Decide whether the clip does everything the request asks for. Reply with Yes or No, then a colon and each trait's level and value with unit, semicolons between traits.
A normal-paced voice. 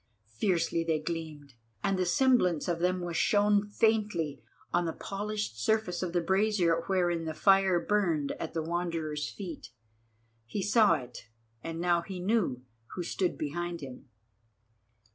Yes: average, 145 wpm